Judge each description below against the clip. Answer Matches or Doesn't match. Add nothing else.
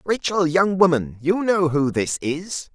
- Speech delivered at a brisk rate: Doesn't match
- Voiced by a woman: Doesn't match